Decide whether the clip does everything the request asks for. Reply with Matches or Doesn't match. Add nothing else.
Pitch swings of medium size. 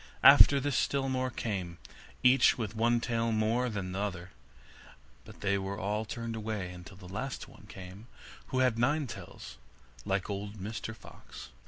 Matches